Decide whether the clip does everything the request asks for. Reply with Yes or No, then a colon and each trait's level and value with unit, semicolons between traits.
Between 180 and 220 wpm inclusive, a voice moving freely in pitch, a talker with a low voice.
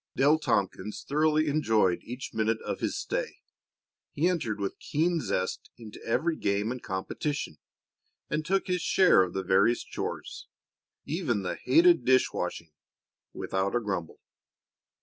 No: average, 140 wpm; wide, 7.8 semitones; low, 120 Hz